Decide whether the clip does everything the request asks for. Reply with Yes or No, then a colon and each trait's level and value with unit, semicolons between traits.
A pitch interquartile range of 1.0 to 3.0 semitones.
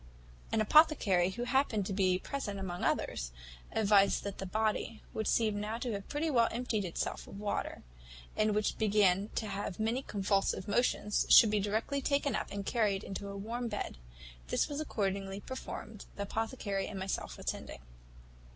Yes: average, 2.7 semitones